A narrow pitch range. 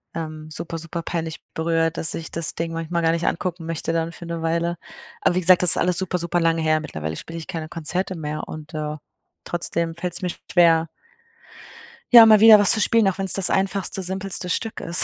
Yes: narrow, 1.8 semitones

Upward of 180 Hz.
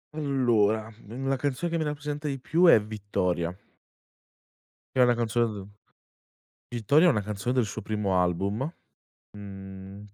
No: low, 110 Hz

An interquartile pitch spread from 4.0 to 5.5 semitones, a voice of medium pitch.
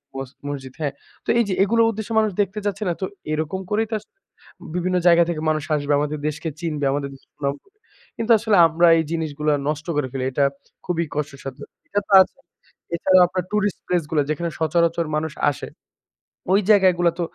Yes: average, 4.4 semitones; medium, 170 Hz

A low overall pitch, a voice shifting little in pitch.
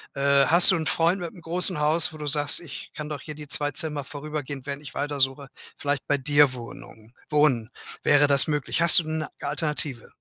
No: medium, 145 Hz; narrow, 1.9 semitones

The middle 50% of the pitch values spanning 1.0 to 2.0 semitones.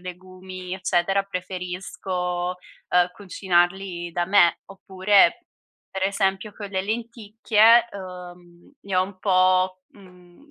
Yes: narrow, 1.7 semitones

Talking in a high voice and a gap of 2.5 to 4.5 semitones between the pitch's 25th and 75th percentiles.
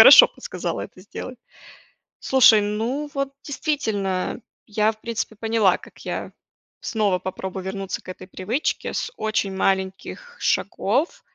No: high, 215 Hz; average, 4.9 semitones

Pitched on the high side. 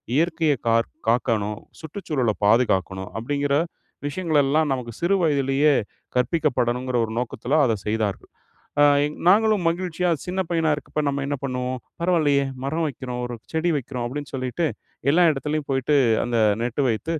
No: medium, 140 Hz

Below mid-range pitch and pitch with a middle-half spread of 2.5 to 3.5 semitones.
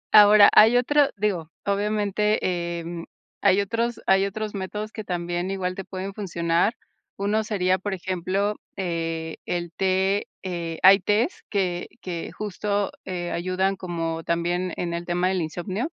No: high, 190 Hz; average, 2.9 semitones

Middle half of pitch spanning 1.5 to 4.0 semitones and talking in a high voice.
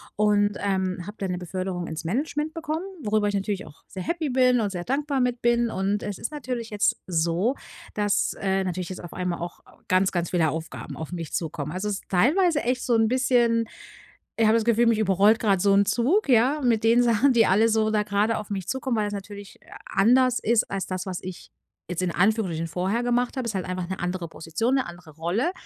No: average, 4.5 semitones; high, 205 Hz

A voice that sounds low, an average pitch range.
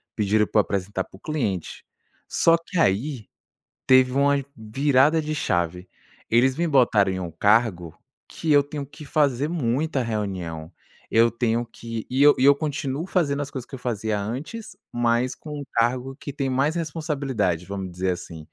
No: low, 125 Hz; wide, 5.8 semitones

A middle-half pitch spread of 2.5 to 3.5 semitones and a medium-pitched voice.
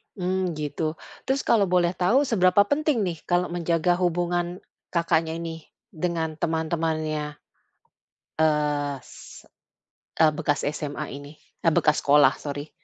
Yes: average, 2.8 semitones; medium, 165 Hz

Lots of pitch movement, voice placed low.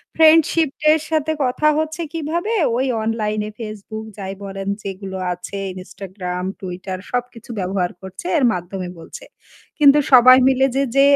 No: wide, 6.7 semitones; high, 220 Hz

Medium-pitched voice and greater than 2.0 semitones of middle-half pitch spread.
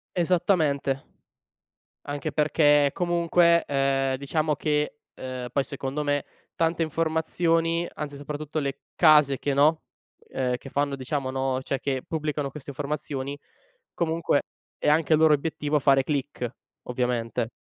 Yes: medium, 145 Hz; narrow, 2.6 semitones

